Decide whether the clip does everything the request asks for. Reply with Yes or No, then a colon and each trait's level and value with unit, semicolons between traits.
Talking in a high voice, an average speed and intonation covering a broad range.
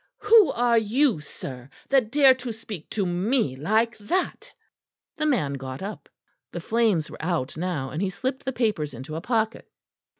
Yes: high, 215 Hz; average, 170 wpm; wide, 8.0 semitones